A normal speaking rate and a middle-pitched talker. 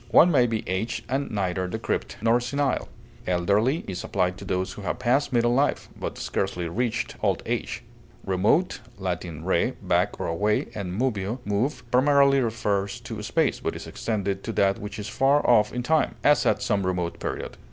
No: average, 180 wpm; low, 110 Hz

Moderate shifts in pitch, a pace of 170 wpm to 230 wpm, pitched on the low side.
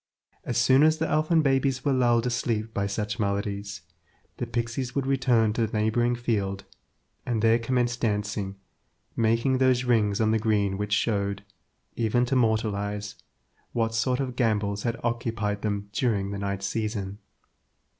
No: average, 3.1 semitones; average, 155 wpm; low, 115 Hz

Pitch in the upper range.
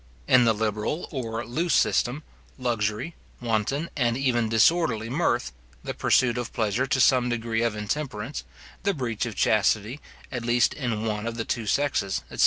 No: low, 120 Hz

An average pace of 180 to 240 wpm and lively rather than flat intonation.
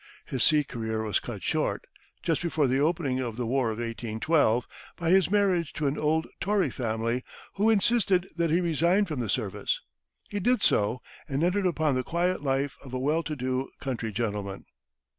Yes: average, 185 wpm; wide, 6.2 semitones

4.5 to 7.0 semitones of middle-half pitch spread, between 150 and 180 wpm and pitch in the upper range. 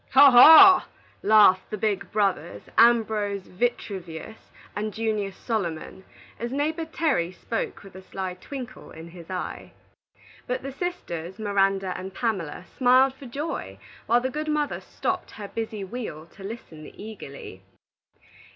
No: average, 5.1 semitones; slow, 135 wpm; high, 210 Hz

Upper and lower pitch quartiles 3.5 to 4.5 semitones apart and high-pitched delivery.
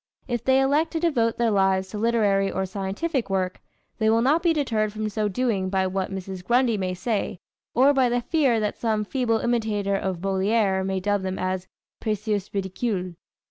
Yes: average, 3.8 semitones; high, 210 Hz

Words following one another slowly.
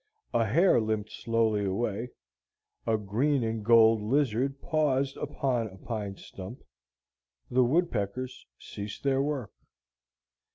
Yes: slow, 115 wpm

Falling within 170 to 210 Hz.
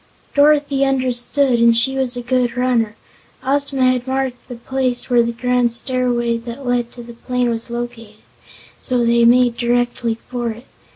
No: high, 245 Hz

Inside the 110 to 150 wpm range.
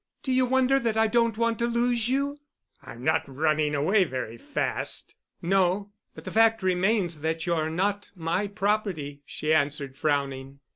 No: average, 160 wpm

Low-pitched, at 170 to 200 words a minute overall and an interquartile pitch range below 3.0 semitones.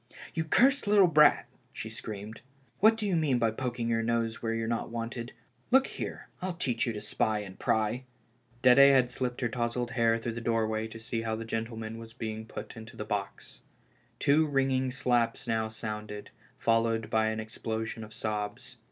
Yes: low, 115 Hz; average, 185 wpm; narrow, 2.4 semitones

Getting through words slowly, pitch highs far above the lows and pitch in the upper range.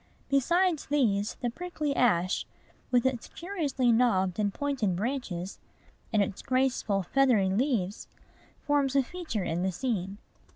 Yes: slow, 130 wpm; wide, 5.9 semitones; high, 245 Hz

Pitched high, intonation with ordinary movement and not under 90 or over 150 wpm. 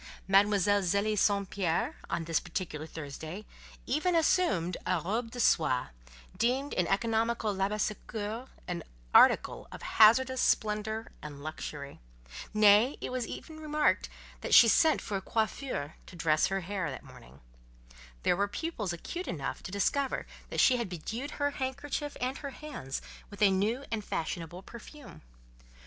No: high, 210 Hz; wide, 6.0 semitones; average, 145 wpm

